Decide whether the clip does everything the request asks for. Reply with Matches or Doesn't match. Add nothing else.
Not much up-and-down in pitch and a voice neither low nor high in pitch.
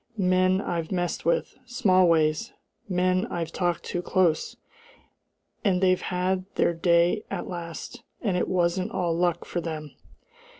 Matches